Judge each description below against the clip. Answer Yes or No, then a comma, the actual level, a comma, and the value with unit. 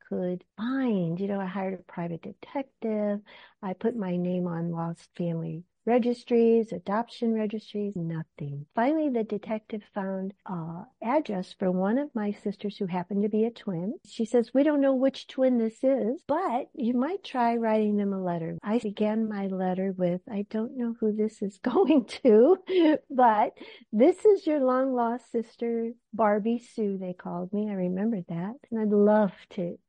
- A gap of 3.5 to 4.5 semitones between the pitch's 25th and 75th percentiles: Yes, average, 4.0 semitones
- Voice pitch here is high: Yes, high, 215 Hz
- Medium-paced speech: Yes, average, 175 wpm